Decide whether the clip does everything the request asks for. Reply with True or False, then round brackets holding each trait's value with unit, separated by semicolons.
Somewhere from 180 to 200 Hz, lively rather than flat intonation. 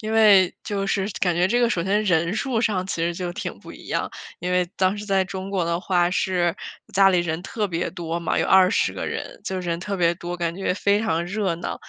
False (185 Hz; 2.4 semitones)